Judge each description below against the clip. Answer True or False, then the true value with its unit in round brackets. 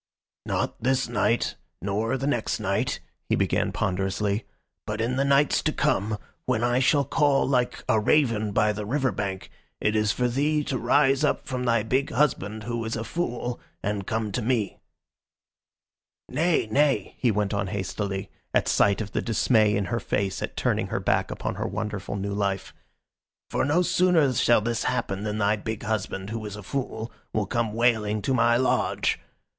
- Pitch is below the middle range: True (110 Hz)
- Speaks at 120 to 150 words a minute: False (180 wpm)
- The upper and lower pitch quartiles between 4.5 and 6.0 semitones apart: False (3.6 semitones)